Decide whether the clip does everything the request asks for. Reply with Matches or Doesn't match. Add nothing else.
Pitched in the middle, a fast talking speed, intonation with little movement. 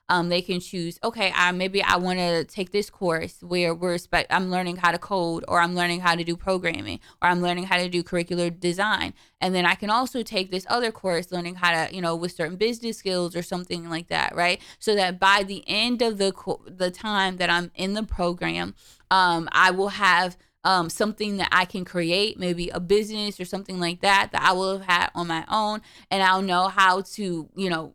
Matches